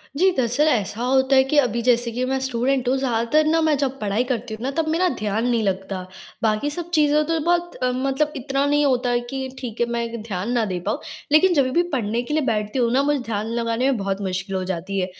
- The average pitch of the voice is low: No, very high, 250 Hz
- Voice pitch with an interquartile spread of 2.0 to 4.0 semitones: No, average, 4.6 semitones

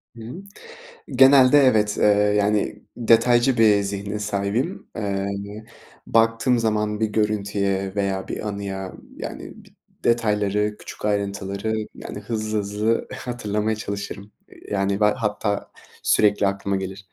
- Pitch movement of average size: No, narrow, 1.9 semitones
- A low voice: Yes, low, 105 Hz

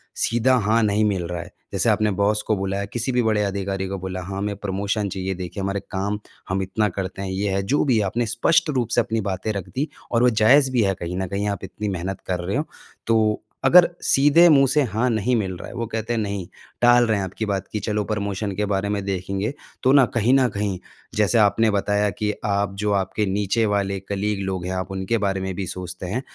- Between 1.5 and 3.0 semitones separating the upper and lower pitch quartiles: Yes, average, 2.7 semitones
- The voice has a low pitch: Yes, low, 100 Hz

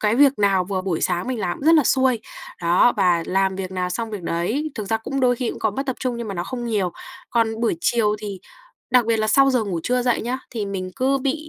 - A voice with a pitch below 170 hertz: No, high, 220 Hz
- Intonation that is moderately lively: Yes, average, 4.8 semitones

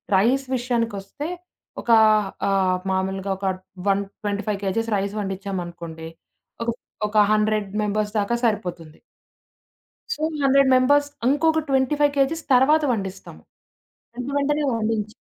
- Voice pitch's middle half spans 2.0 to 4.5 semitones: No, average, 5.3 semitones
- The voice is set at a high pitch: Yes, high, 215 Hz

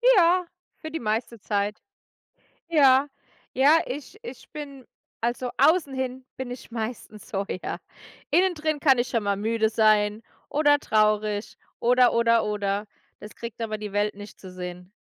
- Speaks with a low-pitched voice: No, high, 230 Hz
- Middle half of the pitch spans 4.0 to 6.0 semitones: Yes, average, 4.7 semitones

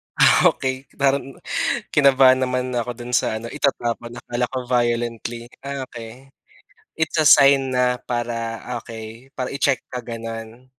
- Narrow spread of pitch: Yes, narrow, 2.3 semitones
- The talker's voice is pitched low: Yes, low, 125 Hz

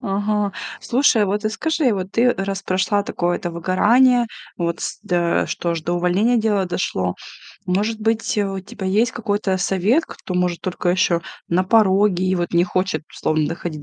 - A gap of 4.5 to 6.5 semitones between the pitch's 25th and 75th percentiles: No, average, 3.4 semitones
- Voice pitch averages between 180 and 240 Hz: Yes, high, 190 Hz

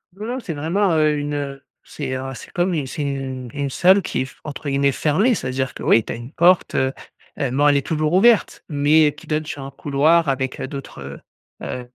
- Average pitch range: Yes, average, 3.2 semitones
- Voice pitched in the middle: Yes, medium, 145 Hz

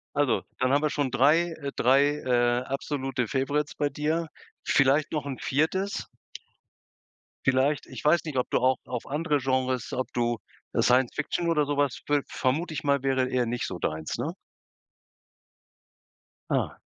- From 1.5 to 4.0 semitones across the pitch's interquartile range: Yes, narrow, 2.6 semitones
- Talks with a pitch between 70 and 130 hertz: No, medium, 140 Hz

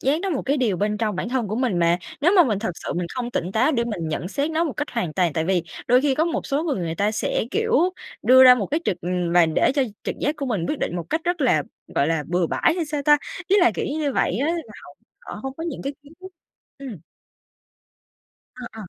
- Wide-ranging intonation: Yes, wide, 8.4 semitones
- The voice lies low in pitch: No, very high, 250 Hz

